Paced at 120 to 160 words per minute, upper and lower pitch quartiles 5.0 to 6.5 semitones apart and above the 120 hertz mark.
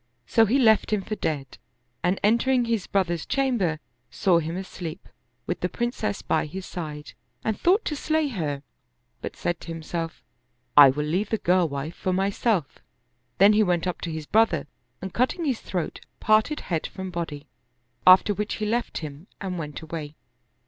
No: average, 175 wpm; average, 5.3 semitones; medium, 185 Hz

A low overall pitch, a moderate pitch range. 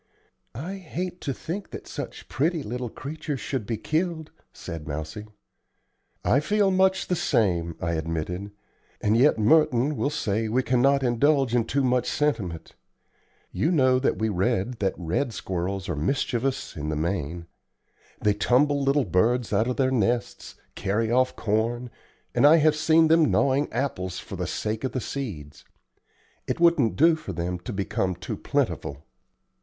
No: low, 120 Hz; wide, 7.1 semitones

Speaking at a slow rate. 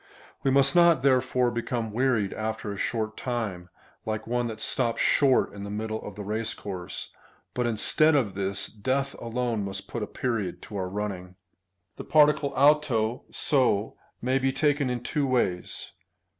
No: average, 165 wpm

